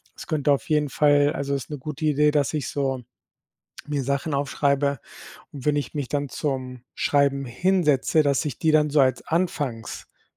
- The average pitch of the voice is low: No, medium, 145 Hz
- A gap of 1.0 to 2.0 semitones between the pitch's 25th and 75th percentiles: Yes, narrow, 1.7 semitones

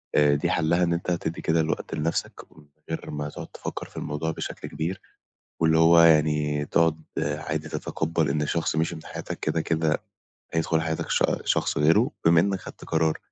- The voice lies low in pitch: Yes, very low, 80 Hz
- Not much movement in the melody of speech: Yes, narrow, 1.3 semitones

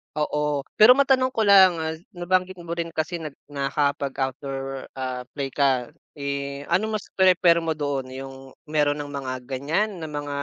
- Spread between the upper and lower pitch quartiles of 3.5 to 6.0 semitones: Yes, average, 4.1 semitones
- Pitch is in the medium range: Yes, medium, 145 Hz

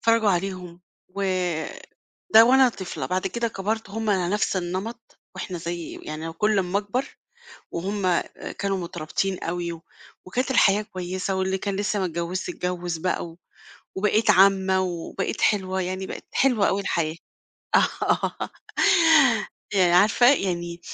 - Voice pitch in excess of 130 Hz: Yes, high, 190 Hz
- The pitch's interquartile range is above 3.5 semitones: No, average, 2.9 semitones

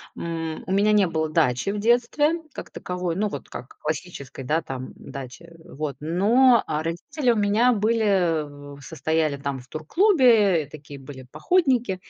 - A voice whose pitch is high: No, medium, 170 Hz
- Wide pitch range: Yes, wide, 6.4 semitones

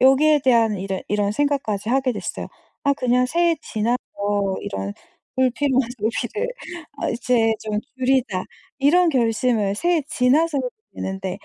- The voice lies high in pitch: Yes, very high, 250 Hz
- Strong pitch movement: No, average, 4.5 semitones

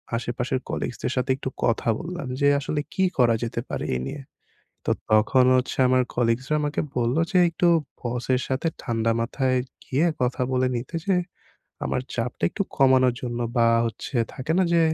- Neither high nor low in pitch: No, low, 130 Hz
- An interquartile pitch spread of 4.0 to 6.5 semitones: No, average, 2.9 semitones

